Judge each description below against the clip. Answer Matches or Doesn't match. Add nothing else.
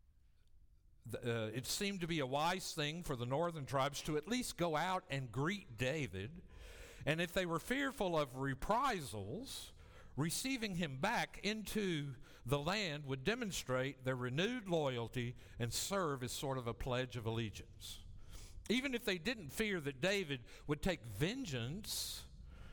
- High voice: Doesn't match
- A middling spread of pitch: Doesn't match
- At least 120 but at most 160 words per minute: Matches